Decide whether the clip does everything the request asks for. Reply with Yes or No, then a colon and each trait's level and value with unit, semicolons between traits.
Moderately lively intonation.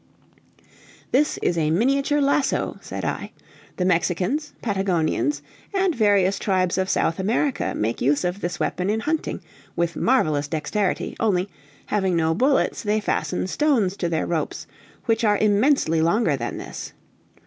No: wide, 5.8 semitones